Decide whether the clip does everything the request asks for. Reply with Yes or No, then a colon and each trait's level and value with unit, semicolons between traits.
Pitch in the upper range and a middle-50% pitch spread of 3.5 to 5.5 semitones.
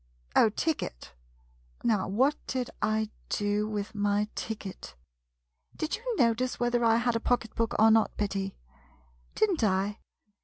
No: high, 220 Hz; average, 2.9 semitones